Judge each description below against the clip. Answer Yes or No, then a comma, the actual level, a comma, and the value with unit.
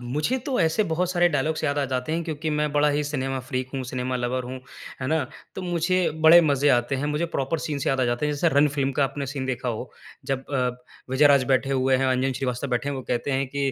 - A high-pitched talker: No, low, 135 Hz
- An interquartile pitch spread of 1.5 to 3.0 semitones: Yes, narrow, 2.6 semitones